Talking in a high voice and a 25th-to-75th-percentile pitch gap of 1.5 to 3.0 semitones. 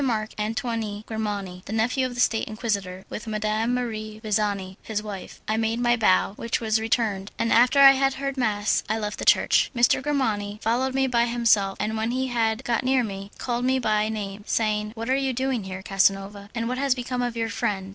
Yes: high, 220 Hz; average, 2.7 semitones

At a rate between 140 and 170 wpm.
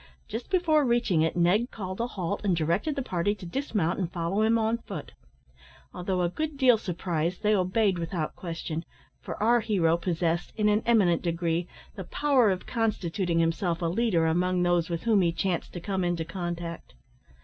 No: average, 180 wpm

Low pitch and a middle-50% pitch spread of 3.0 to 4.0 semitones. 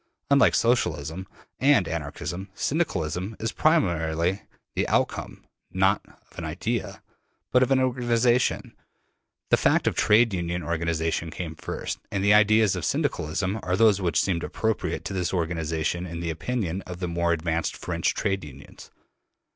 No: very low, 90 Hz; average, 4.8 semitones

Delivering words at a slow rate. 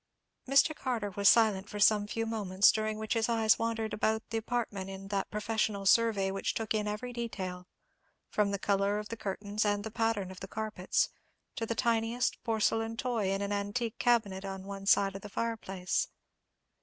No: average, 185 wpm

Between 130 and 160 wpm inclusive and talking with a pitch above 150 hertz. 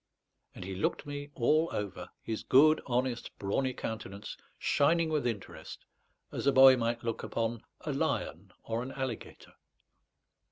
No: average, 145 wpm; low, 125 Hz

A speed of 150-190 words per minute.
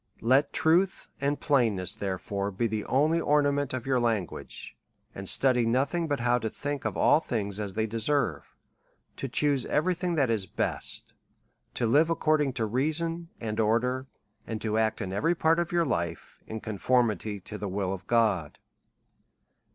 Yes: average, 175 wpm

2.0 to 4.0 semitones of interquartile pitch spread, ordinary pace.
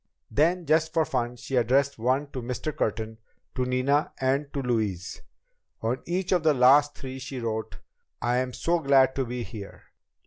Yes: average, 3.3 semitones; average, 170 wpm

